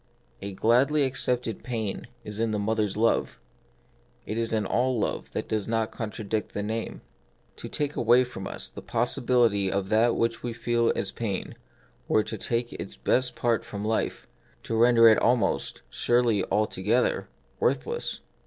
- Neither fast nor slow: Yes, average, 165 wpm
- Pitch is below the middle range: Yes, low, 115 Hz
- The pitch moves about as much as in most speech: No, narrow, 2.3 semitones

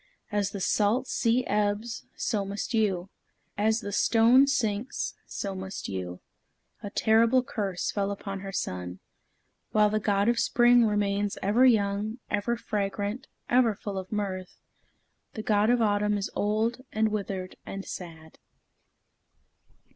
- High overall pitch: Yes, high, 205 Hz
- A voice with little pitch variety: Yes, narrow, 2.3 semitones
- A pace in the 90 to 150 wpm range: Yes, average, 140 wpm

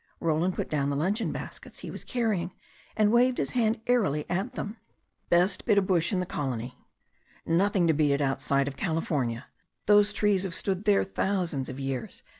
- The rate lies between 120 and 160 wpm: No, average, 185 wpm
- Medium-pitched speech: Yes, medium, 180 Hz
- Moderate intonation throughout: No, wide, 6.4 semitones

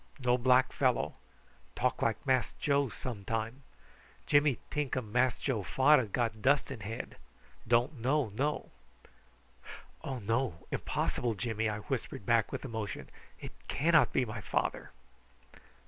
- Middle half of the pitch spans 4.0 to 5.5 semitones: No, average, 3.4 semitones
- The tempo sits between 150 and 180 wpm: No, slow, 135 wpm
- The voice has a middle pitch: No, low, 125 Hz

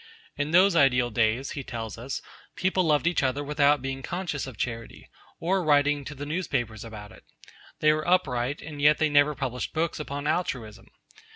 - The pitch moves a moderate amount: Yes, average, 3.6 semitones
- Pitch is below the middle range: No, medium, 145 Hz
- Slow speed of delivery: No, average, 180 wpm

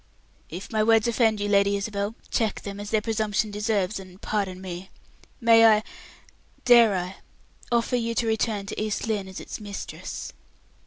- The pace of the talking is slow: No, average, 165 wpm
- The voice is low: No, high, 210 Hz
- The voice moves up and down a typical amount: No, narrow, 2.1 semitones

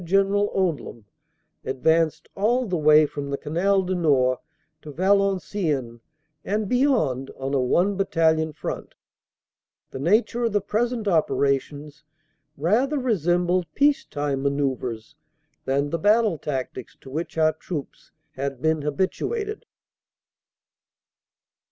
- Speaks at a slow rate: Yes, slow, 115 wpm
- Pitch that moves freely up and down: Yes, wide, 6.0 semitones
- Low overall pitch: No, medium, 160 Hz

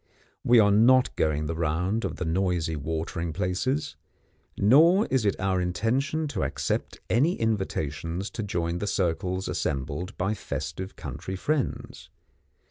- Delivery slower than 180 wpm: Yes, slow, 135 wpm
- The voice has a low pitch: Yes, very low, 95 Hz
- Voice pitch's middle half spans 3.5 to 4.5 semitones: No, wide, 5.4 semitones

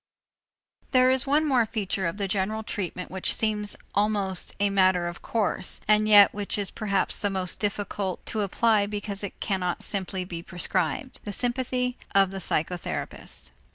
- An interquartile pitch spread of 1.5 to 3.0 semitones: Yes, narrow, 2.4 semitones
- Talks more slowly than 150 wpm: No, average, 155 wpm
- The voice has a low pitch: No, high, 200 Hz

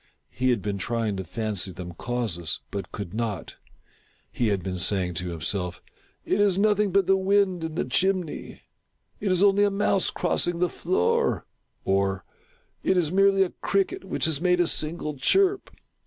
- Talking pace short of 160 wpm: No, average, 185 wpm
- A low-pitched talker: No, medium, 150 Hz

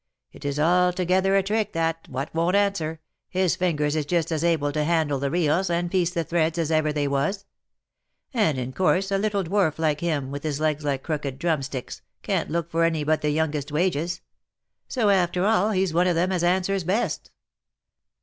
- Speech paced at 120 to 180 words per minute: No, average, 195 wpm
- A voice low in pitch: No, medium, 165 Hz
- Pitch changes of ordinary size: Yes, average, 3.5 semitones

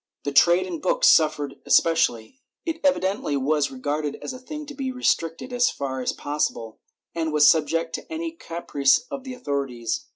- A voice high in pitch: No, medium, 165 Hz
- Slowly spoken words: No, average, 175 wpm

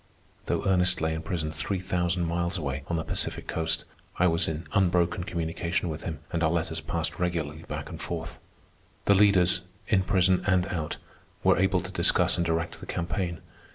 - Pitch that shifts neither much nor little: No, narrow, 2.0 semitones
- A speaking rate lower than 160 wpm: No, average, 185 wpm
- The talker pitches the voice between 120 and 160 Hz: No, very low, 85 Hz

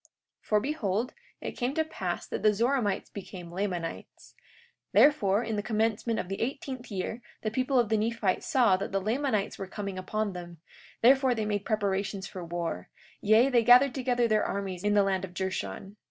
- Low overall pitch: No, high, 210 Hz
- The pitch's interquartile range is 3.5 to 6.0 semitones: Yes, average, 4.0 semitones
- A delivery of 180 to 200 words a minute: Yes, average, 185 wpm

